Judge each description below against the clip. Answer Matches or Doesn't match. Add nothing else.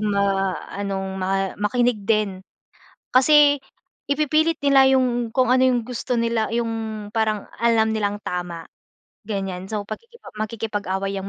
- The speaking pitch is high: Matches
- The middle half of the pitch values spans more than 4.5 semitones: Doesn't match